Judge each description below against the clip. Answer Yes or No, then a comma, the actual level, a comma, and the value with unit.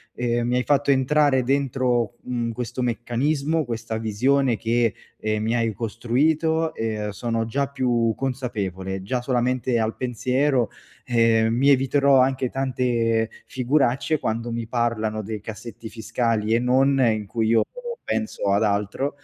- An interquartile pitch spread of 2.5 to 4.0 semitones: Yes, average, 2.8 semitones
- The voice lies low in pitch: Yes, low, 120 Hz